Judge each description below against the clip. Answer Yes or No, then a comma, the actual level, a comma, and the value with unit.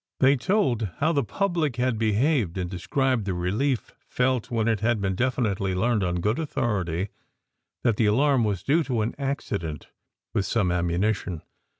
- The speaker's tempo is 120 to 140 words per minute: No, average, 165 wpm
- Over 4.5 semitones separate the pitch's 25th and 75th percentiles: Yes, wide, 5.4 semitones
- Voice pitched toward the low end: Yes, low, 110 Hz